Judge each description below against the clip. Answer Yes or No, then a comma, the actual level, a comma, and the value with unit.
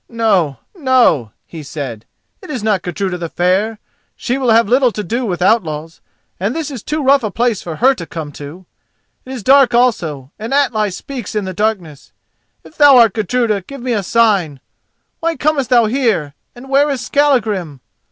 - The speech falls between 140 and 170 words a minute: No, average, 185 wpm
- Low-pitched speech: No, high, 220 Hz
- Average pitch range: No, wide, 6.5 semitones